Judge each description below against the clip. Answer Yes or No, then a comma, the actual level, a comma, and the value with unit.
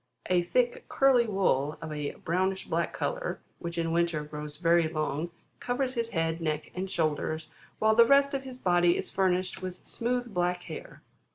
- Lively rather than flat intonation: Yes, wide, 6.2 semitones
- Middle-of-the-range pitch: Yes, medium, 180 Hz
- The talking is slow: No, average, 175 wpm